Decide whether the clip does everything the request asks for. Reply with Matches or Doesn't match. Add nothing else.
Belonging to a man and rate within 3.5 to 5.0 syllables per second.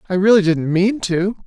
Matches